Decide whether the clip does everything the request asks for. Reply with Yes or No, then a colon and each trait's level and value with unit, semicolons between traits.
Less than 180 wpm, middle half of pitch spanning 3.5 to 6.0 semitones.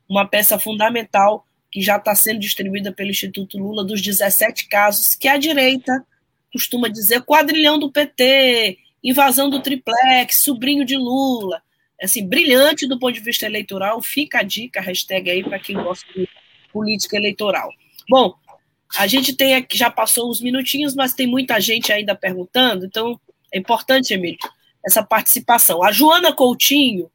Yes: average, 155 wpm; average, 4.8 semitones